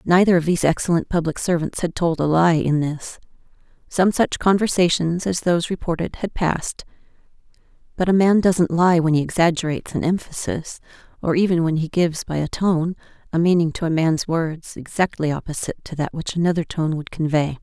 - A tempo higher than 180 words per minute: No, average, 175 wpm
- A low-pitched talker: No, medium, 170 Hz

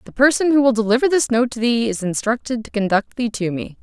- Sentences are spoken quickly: Yes, fast, 250 wpm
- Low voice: No, high, 235 Hz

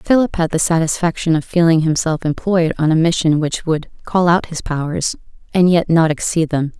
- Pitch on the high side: No, medium, 165 Hz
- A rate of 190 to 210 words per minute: Yes, average, 195 wpm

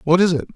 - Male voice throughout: Yes, male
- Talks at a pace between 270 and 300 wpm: No, fast, 325 wpm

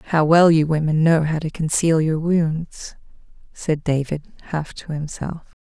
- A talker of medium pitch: Yes, medium, 160 Hz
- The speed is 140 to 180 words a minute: Yes, average, 160 wpm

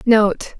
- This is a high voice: Yes, high, 215 Hz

